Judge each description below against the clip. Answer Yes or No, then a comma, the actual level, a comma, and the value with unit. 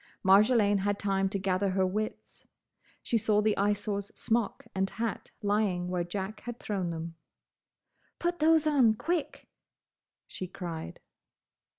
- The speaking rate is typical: No, slow, 130 wpm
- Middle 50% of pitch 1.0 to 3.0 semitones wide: Yes, narrow, 2.5 semitones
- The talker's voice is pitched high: Yes, high, 205 Hz